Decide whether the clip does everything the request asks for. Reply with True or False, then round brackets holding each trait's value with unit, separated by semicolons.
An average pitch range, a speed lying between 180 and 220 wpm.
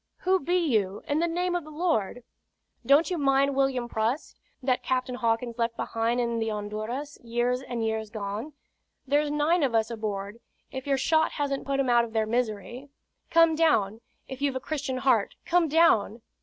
True (4.6 semitones; 185 wpm)